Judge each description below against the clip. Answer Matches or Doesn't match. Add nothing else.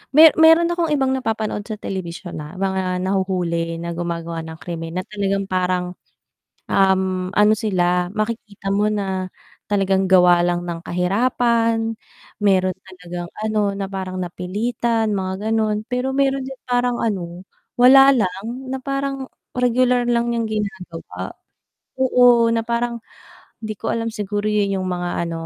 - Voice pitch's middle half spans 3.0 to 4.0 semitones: Doesn't match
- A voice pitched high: Matches